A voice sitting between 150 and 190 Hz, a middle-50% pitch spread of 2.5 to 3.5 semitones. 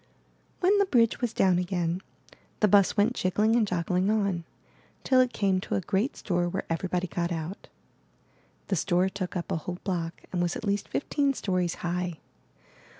Yes: medium, 185 Hz; average, 3.2 semitones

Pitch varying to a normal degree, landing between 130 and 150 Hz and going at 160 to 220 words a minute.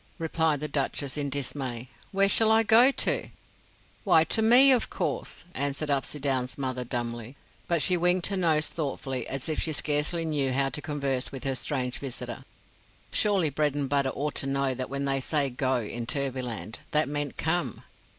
Yes: average, 3.4 semitones; medium, 140 Hz; average, 170 wpm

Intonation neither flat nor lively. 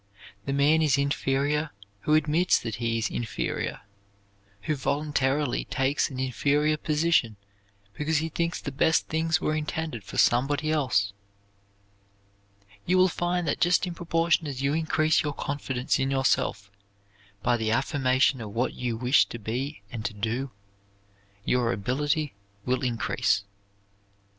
Yes: average, 3.9 semitones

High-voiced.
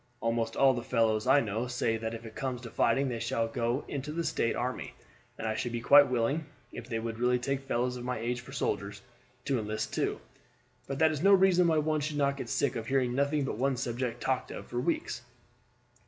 No: low, 125 Hz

